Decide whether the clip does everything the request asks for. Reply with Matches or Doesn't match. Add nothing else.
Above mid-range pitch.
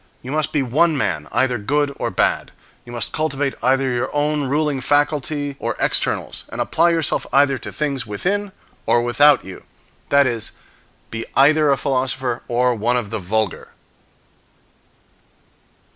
Doesn't match